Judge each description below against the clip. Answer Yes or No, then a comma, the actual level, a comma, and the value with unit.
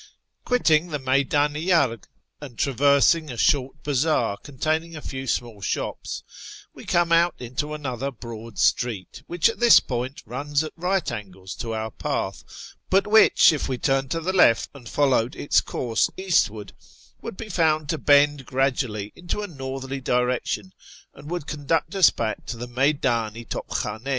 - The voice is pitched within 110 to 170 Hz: Yes, medium, 140 Hz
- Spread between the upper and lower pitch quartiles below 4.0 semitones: No, average, 4.6 semitones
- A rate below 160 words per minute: No, average, 165 wpm